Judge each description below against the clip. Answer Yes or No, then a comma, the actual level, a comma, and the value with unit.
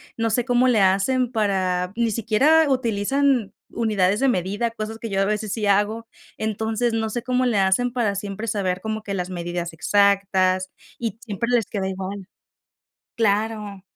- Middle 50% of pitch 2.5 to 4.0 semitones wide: Yes, average, 3.1 semitones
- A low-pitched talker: No, high, 215 Hz